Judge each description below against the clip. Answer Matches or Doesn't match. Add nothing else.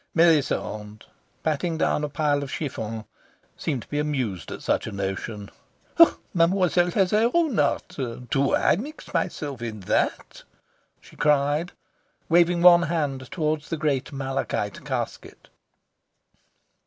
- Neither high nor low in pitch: Matches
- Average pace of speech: Doesn't match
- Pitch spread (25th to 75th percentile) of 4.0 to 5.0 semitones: Matches